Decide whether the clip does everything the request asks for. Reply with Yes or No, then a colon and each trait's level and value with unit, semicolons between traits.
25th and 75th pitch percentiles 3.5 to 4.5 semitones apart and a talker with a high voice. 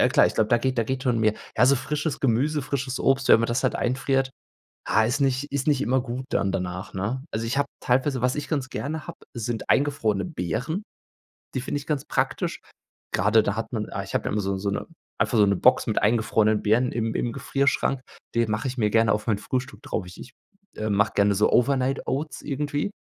No: average, 4.0 semitones; low, 125 Hz